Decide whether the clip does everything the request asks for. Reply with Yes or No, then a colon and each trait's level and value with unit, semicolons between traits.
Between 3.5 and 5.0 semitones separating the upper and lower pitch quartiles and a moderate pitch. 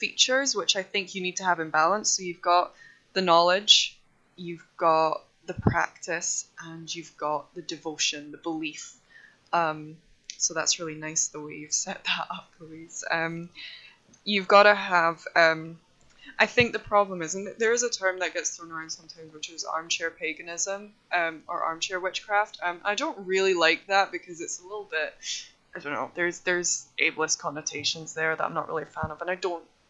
No: average, 3.1 semitones; medium, 170 Hz